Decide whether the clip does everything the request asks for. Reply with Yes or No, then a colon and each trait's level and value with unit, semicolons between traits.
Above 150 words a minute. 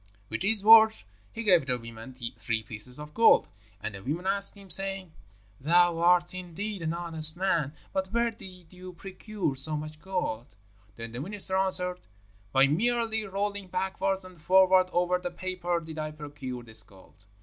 Yes: average, 170 wpm